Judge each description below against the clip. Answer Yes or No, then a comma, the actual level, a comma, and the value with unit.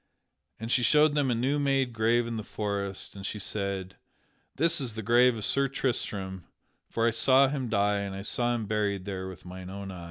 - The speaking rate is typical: No, fast, 215 wpm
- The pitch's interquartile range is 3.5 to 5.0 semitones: Yes, average, 4.3 semitones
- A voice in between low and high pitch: No, low, 110 Hz